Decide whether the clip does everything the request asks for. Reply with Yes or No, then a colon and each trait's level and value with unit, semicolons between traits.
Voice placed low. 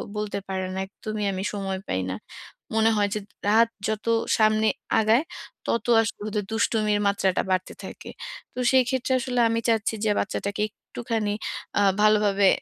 No: high, 215 Hz